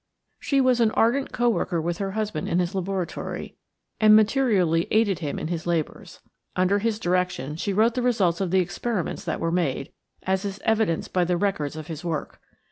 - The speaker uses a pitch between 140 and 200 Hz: Yes, high, 190 Hz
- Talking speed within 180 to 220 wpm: Yes, average, 195 wpm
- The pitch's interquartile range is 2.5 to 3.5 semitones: No, average, 4.3 semitones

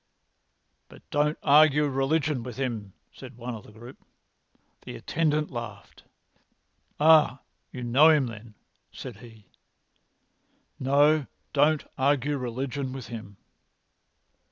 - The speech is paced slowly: Yes, slow, 110 wpm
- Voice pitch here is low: Yes, low, 130 Hz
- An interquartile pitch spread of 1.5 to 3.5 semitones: No, average, 3.9 semitones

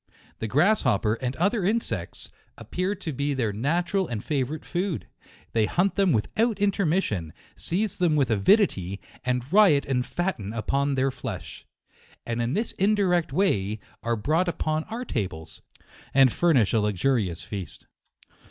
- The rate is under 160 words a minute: Yes, average, 145 wpm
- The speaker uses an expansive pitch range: Yes, wide, 8.6 semitones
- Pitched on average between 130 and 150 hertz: Yes, medium, 140 Hz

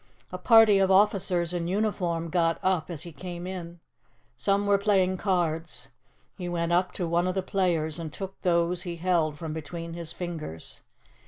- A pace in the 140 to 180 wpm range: Yes, average, 175 wpm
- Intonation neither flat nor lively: No, narrow, 2.1 semitones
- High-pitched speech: No, medium, 175 Hz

